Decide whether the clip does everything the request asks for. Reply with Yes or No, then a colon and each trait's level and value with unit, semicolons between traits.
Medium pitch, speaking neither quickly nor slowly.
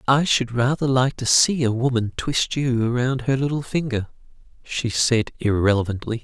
No: low, 125 Hz; average, 165 wpm